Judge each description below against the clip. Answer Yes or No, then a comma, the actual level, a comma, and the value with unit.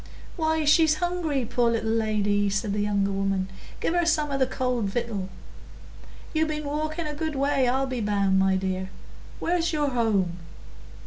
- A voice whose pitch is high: Yes, high, 245 Hz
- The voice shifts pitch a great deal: Yes, wide, 7.1 semitones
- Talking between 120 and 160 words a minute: No, average, 170 wpm